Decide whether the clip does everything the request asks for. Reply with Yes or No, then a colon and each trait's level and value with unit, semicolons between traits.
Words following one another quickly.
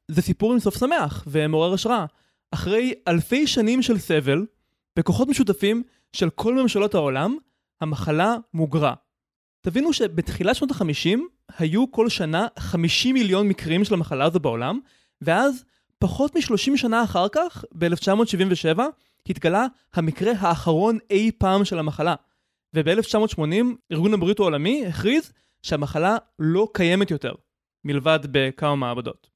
No: average, 125 wpm